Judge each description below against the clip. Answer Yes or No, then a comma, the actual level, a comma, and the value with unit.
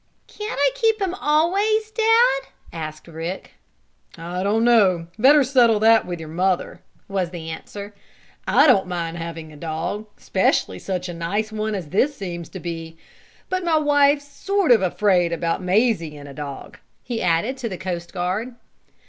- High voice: Yes, high, 195 Hz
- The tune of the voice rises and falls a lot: Yes, wide, 8.1 semitones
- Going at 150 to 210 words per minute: Yes, average, 165 wpm